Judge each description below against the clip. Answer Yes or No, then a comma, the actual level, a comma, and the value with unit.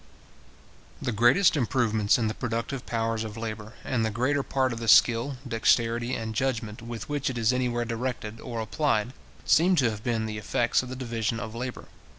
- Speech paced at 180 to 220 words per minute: Yes, average, 185 wpm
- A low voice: Yes, low, 115 Hz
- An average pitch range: No, narrow, 2.3 semitones